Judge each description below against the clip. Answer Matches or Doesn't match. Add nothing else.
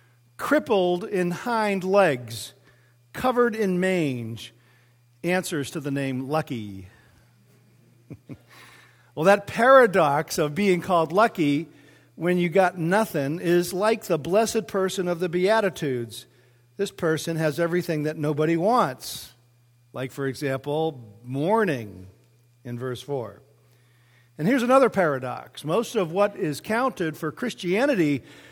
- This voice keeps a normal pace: Doesn't match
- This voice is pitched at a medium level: Matches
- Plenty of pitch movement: Matches